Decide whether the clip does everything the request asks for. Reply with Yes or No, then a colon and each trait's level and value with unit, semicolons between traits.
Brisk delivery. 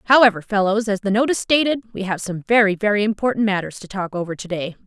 Yes: fast, 220 wpm